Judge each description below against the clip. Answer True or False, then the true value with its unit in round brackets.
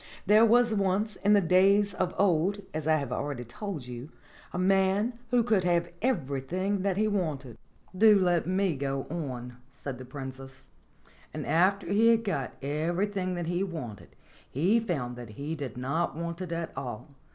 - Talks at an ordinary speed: True (175 wpm)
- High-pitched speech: False (175 Hz)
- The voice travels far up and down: True (6.3 semitones)